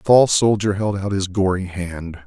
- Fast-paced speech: Yes, fast, 210 wpm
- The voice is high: No, very low, 95 Hz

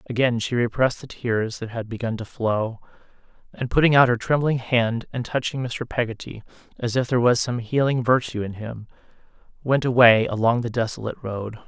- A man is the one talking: Yes, male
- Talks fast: No, average, 180 wpm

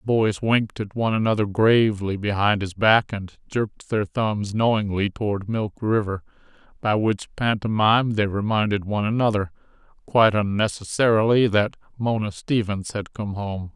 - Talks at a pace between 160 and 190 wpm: No, average, 140 wpm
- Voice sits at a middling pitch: No, low, 105 Hz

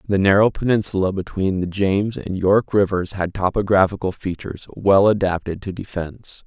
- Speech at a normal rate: Yes, average, 150 wpm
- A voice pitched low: Yes, very low, 95 Hz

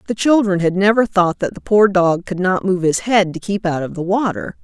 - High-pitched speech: Yes, high, 195 Hz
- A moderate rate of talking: No, fast, 260 wpm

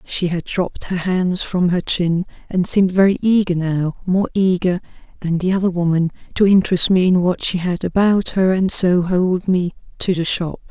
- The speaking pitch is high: No, medium, 180 Hz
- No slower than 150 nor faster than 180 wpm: No, average, 195 wpm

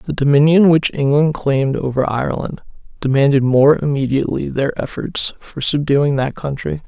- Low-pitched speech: No, medium, 145 Hz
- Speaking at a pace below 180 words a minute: Yes, average, 140 wpm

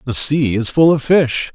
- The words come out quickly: Yes, fast, 235 wpm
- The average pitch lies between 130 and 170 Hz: Yes, medium, 140 Hz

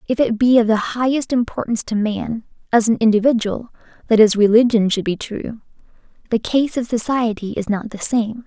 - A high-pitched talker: Yes, high, 225 Hz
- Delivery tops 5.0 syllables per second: Yes, 5.3 syllables/s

